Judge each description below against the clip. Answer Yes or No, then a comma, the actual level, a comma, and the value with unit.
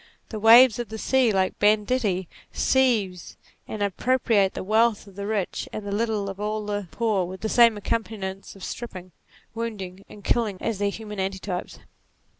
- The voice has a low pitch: No, high, 210 Hz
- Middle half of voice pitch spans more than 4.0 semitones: No, average, 2.7 semitones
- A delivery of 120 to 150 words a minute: No, average, 175 wpm